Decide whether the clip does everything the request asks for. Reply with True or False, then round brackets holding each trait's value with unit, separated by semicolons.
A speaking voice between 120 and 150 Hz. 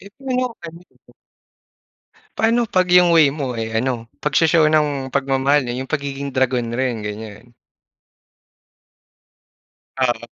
True (135 Hz)